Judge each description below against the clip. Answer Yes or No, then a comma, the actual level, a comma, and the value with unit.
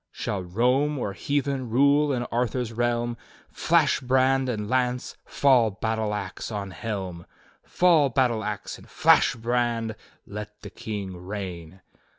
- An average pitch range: Yes, average, 3.8 semitones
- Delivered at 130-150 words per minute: Yes, slow, 135 wpm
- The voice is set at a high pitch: No, low, 115 Hz